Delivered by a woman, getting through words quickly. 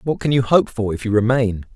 No: male; fast, 275 wpm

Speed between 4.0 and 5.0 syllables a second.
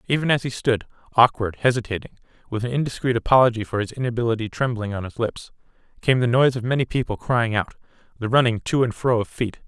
No: 6.4 syllables/s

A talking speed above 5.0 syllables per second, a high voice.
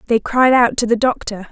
Yes: 5.3 syllables/s; high, 235 Hz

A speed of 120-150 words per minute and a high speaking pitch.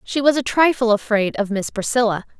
No: average, 200 wpm; high, 235 Hz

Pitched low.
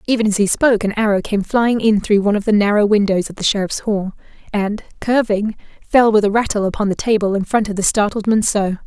No: high, 210 Hz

